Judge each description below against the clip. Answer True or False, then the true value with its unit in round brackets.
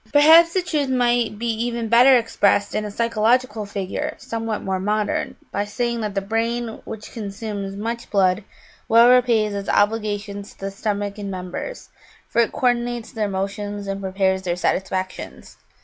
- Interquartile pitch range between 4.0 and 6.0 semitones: False (2.9 semitones)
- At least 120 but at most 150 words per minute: False (165 wpm)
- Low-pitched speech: False (215 Hz)